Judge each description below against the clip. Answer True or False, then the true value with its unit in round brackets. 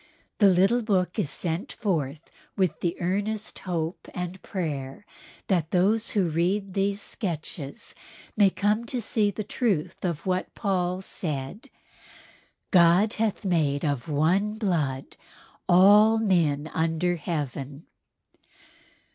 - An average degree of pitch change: True (4.2 semitones)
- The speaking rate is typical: False (120 wpm)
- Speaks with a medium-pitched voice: True (180 Hz)